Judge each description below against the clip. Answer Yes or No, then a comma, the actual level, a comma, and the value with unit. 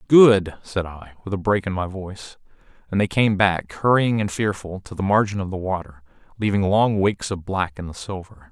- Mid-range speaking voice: No, very low, 95 Hz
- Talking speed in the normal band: No, fast, 210 wpm